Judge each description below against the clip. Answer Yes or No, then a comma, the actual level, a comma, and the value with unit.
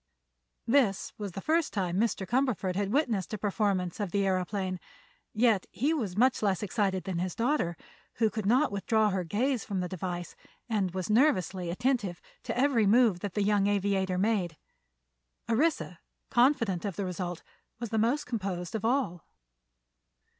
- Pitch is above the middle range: Yes, high, 205 Hz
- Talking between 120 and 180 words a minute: Yes, average, 160 wpm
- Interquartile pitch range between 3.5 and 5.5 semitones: Yes, average, 4.0 semitones